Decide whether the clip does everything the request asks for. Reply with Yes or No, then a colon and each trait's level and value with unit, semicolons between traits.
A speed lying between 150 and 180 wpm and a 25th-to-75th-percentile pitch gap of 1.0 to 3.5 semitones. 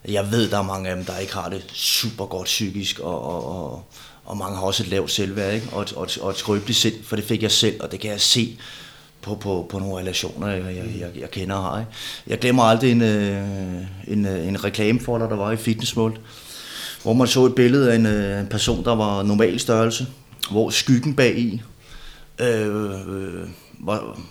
No: average, 210 wpm; average, 2.9 semitones